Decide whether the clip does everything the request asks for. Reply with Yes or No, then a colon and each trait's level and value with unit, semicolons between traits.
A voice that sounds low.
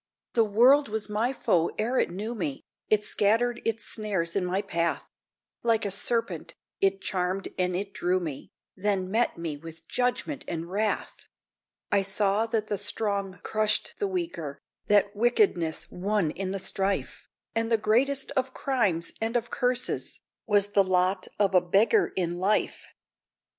No: high, 205 Hz